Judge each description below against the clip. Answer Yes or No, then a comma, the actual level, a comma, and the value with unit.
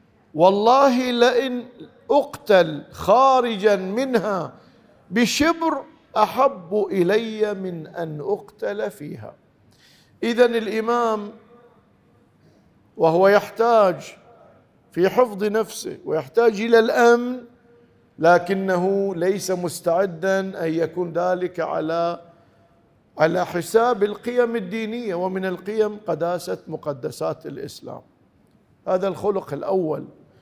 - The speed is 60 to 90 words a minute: Yes, average, 80 wpm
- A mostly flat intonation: No, average, 4.8 semitones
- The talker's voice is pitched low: No, high, 205 Hz